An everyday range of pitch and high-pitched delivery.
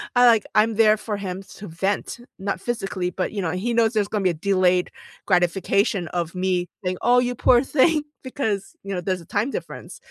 Yes: average, 3.8 semitones; high, 200 Hz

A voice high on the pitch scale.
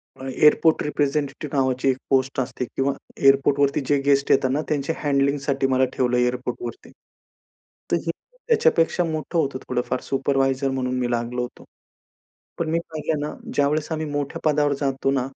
No: medium, 140 Hz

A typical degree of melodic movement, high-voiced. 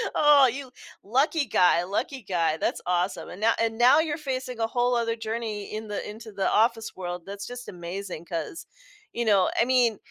Yes: average, 4.1 semitones; high, 225 Hz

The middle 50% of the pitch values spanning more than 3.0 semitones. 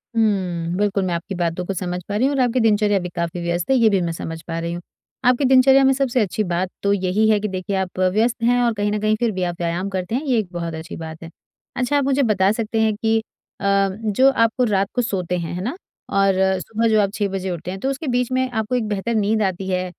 Yes: average, 4.1 semitones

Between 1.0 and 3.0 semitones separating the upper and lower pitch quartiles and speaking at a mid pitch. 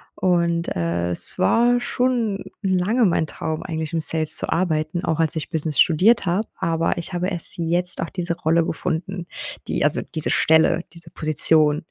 Yes: narrow, 2.4 semitones; medium, 170 Hz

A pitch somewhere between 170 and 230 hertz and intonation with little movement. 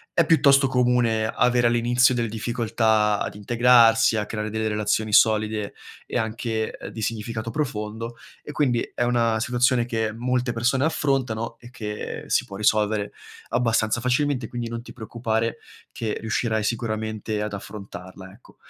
No: low, 115 Hz; narrow, 2.1 semitones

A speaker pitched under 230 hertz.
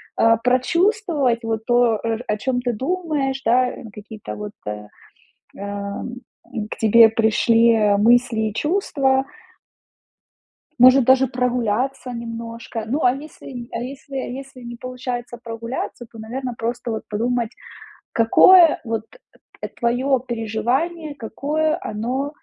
No: high, 245 Hz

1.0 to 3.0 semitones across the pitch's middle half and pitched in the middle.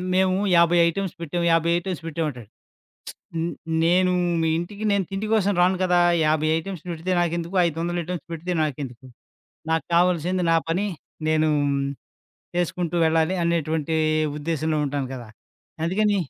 Yes: narrow, 2.4 semitones; medium, 170 Hz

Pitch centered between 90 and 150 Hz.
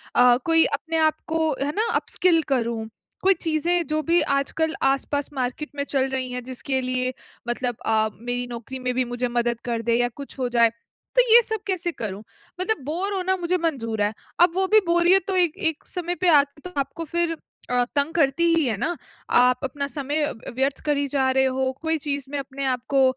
No: very high, 280 Hz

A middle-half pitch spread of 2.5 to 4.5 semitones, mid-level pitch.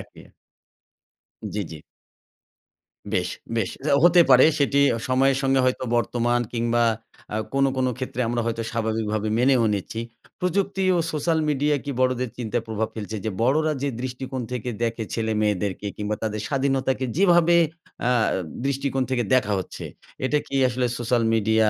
No: average, 3.6 semitones; low, 125 Hz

